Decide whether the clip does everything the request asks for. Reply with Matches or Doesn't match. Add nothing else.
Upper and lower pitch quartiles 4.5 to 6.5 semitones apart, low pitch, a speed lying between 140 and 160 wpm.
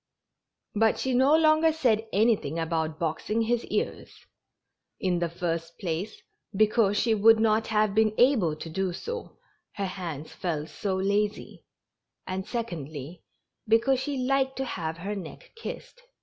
Doesn't match